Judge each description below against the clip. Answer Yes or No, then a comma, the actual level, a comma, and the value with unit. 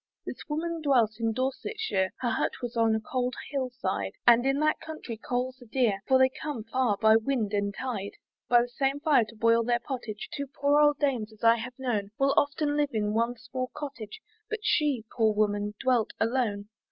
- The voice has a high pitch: Yes, high, 245 Hz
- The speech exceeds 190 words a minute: Yes, average, 200 wpm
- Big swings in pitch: No, average, 3.8 semitones